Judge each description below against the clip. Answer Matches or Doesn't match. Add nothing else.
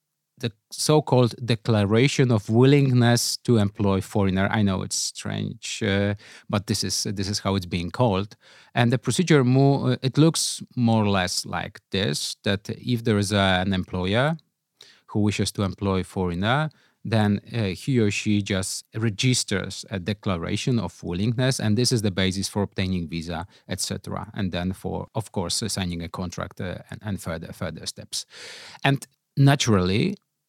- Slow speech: Doesn't match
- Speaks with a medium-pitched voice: Doesn't match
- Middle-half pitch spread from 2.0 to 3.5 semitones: Doesn't match